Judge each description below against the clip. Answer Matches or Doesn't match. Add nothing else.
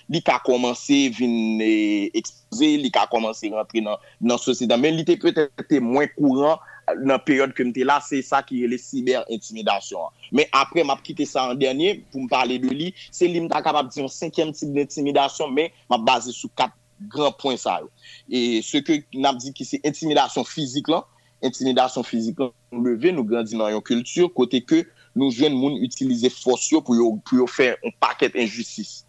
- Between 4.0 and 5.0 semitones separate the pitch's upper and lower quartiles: Matches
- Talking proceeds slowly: Doesn't match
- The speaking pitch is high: Doesn't match